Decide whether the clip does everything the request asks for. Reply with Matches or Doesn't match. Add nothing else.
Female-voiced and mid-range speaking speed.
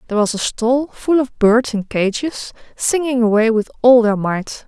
Matches